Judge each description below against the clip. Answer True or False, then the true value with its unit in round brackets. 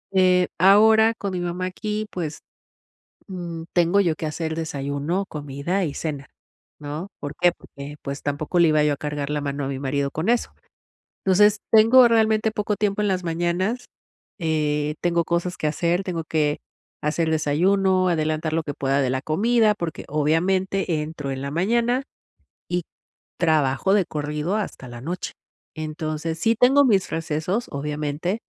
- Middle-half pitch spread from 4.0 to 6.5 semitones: True (4.4 semitones)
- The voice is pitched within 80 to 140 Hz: False (165 Hz)